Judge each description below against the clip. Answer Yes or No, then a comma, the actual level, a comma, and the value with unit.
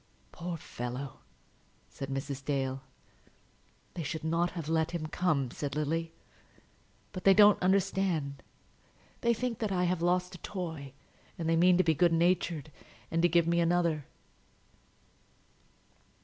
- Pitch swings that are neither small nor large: Yes, average, 3.2 semitones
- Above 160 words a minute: No, average, 140 wpm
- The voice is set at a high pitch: No, medium, 165 Hz